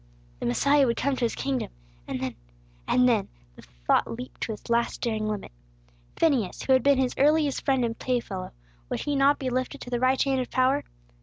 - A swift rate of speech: Yes, fast, 210 wpm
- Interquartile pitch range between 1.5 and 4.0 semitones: Yes, average, 3.1 semitones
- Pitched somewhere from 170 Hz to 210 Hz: No, very high, 255 Hz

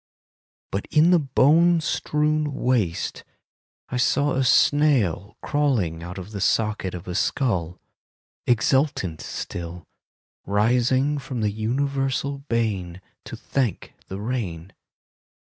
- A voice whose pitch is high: No, low, 120 Hz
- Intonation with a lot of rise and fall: Yes, wide, 6.6 semitones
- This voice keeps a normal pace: No, slow, 110 wpm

